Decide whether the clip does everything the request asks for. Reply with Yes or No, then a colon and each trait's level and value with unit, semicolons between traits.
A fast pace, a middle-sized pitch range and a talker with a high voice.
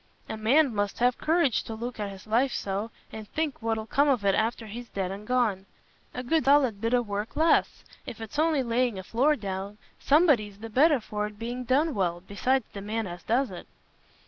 Yes: fast, 210 wpm; average, 4.1 semitones; high, 225 Hz